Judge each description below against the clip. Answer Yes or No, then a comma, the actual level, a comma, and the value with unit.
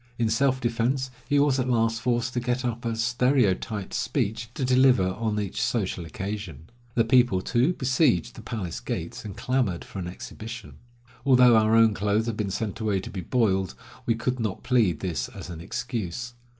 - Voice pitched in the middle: No, low, 115 Hz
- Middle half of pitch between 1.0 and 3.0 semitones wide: No, average, 3.9 semitones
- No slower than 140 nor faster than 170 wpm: No, average, 185 wpm